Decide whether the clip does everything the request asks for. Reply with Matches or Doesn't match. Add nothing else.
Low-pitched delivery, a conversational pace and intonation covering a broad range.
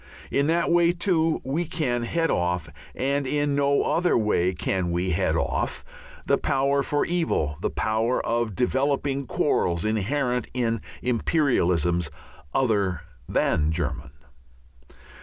Doesn't match